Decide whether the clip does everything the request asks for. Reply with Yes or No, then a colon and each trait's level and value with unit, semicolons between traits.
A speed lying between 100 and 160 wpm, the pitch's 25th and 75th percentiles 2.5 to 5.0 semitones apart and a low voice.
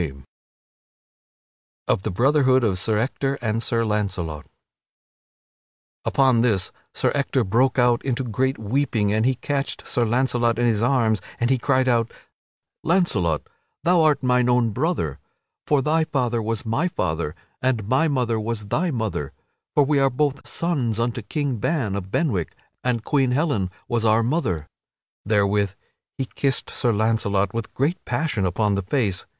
Yes: average, 155 wpm; average, 4.4 semitones; low, 120 Hz